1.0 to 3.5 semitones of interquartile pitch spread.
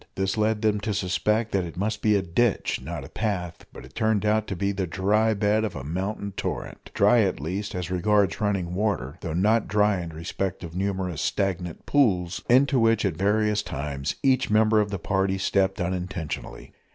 Yes: average, 3.2 semitones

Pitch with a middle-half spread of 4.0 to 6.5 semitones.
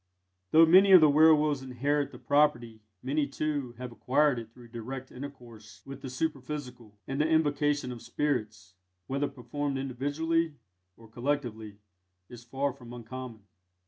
No: average, 3.5 semitones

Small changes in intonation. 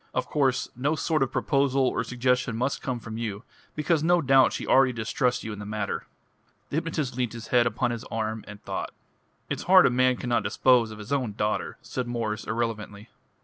No: average, 3.2 semitones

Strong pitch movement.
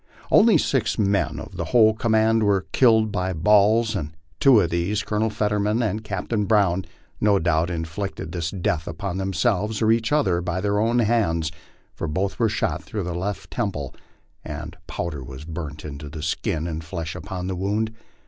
No: average, 4.6 semitones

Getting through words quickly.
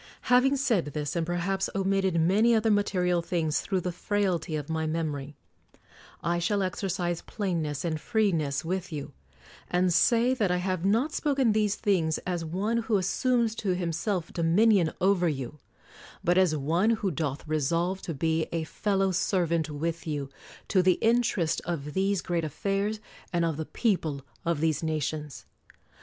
No: average, 160 wpm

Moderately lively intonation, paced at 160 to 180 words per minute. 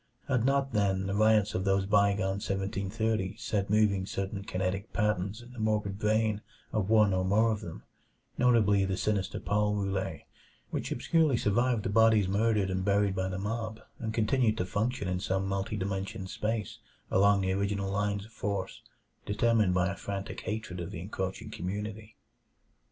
No: narrow, 2.1 semitones; average, 170 wpm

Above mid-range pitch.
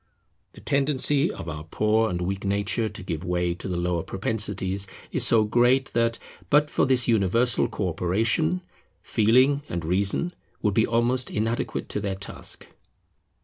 No: low, 105 Hz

